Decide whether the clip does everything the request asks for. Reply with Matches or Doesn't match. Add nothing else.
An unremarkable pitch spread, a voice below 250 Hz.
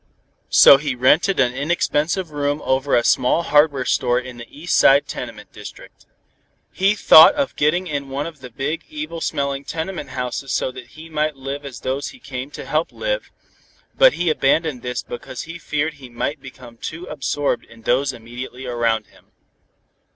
Matches